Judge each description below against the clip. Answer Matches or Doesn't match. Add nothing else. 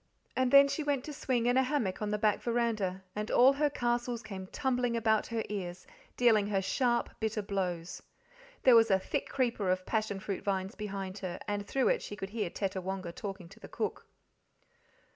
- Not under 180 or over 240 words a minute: Matches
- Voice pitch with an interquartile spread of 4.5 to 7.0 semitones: Doesn't match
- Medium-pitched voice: Doesn't match